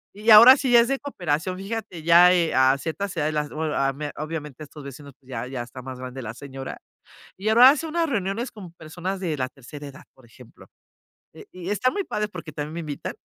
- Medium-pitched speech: Yes, medium, 160 Hz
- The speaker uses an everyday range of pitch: No, wide, 6.7 semitones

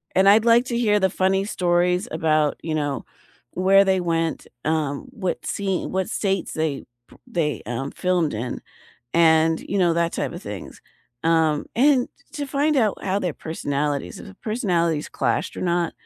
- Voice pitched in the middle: Yes, medium, 175 Hz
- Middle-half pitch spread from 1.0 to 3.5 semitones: No, average, 3.9 semitones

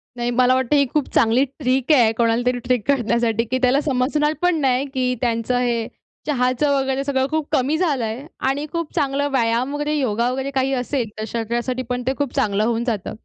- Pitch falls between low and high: No, very high, 255 Hz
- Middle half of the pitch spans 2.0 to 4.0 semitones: Yes, average, 2.8 semitones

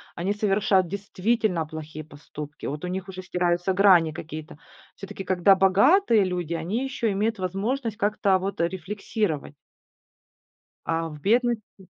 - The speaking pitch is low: No, high, 190 Hz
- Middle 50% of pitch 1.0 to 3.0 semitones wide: No, average, 3.6 semitones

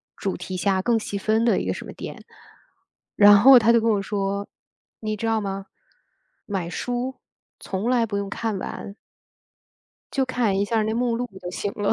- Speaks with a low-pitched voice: No, high, 210 Hz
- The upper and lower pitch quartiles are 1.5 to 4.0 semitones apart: Yes, average, 2.8 semitones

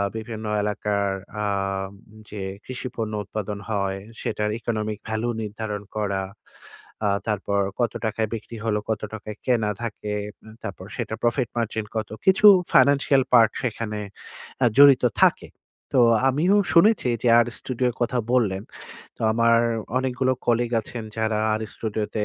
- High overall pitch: No, low, 110 Hz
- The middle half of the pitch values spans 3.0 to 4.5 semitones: No, narrow, 2.6 semitones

